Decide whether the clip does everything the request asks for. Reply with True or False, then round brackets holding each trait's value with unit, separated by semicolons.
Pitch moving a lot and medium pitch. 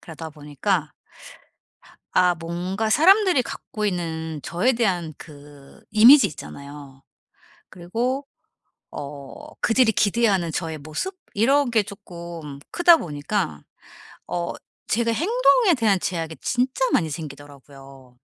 True (7.5 semitones; 180 Hz)